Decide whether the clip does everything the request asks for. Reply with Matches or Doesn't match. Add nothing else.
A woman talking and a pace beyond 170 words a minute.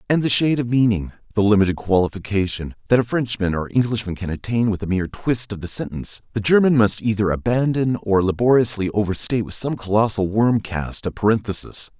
Doesn't match